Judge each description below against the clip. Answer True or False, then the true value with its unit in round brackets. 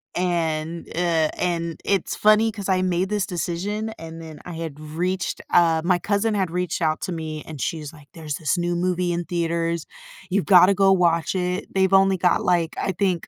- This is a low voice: False (175 Hz)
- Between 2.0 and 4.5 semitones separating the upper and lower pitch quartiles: True (2.4 semitones)